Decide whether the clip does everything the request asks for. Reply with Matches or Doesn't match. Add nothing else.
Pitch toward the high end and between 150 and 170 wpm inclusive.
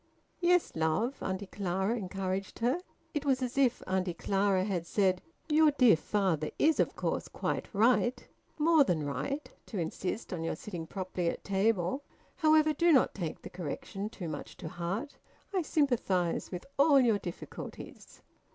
Matches